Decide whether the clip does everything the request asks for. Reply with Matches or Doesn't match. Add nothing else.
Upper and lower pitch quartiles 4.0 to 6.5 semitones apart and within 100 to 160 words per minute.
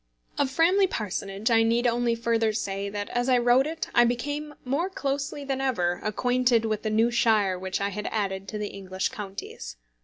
Doesn't match